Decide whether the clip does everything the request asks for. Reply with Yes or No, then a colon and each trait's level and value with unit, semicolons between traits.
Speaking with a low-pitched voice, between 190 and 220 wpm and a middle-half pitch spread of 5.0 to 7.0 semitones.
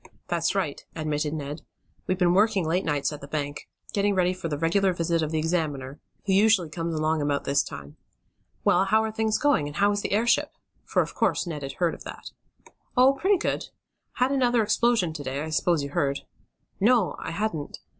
No: medium, 170 Hz; fast, 205 wpm; wide, 5.5 semitones